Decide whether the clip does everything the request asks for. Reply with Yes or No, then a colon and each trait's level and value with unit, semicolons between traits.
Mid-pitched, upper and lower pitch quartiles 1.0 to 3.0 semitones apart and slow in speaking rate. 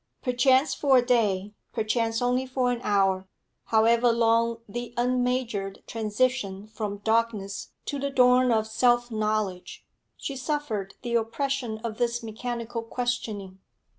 No: high, 235 Hz; narrow, 2.6 semitones; slow, 130 wpm